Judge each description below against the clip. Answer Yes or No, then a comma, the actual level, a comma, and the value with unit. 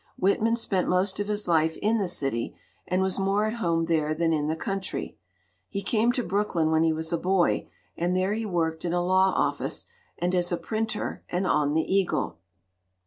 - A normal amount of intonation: Yes, average, 3.5 semitones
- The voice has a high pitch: No, medium, 180 Hz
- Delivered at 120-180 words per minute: No, average, 200 wpm